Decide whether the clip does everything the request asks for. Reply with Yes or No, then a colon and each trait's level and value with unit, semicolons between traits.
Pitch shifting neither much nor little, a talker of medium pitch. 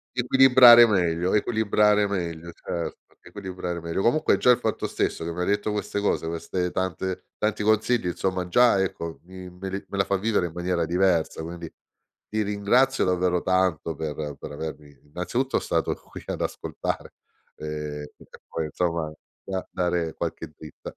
No: average, 3.7 semitones; very low, 90 Hz